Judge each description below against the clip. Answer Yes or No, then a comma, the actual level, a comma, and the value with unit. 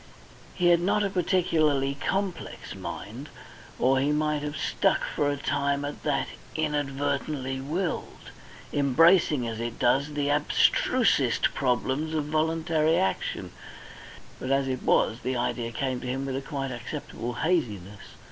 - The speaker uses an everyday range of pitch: Yes, average, 3.2 semitones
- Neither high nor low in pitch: Yes, medium, 145 Hz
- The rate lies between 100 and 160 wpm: Yes, average, 140 wpm